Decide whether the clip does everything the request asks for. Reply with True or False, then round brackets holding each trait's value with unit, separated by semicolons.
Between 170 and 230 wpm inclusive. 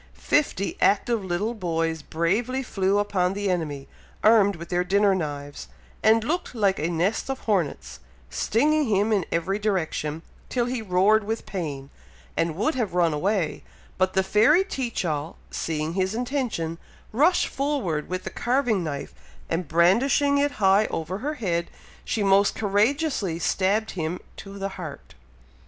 False (150 wpm)